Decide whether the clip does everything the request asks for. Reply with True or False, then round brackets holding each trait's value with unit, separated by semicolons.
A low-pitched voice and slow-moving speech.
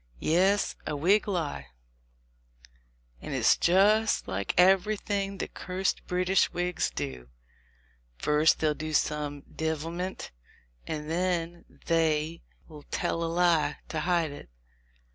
False (165 Hz; 110 wpm)